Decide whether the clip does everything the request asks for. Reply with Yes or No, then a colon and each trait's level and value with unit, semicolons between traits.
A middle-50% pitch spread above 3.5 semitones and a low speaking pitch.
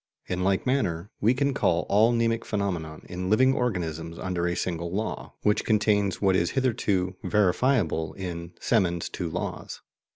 Yes: average, 4.4 semitones; very low, 95 Hz